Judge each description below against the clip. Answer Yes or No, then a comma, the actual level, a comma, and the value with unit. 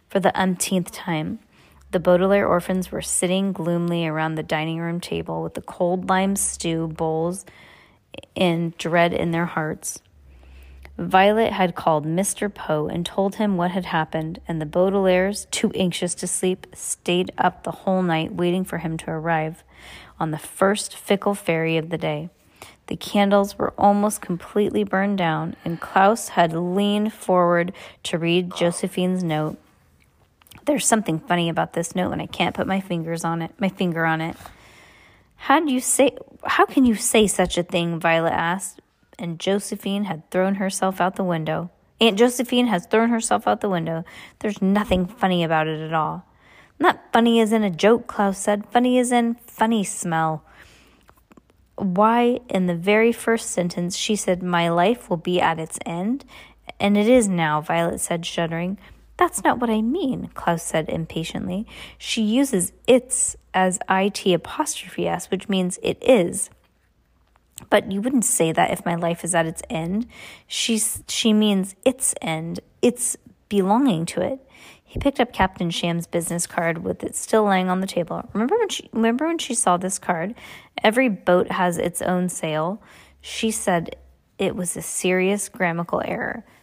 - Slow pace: No, average, 170 wpm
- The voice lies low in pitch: No, medium, 185 Hz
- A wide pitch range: No, average, 3.8 semitones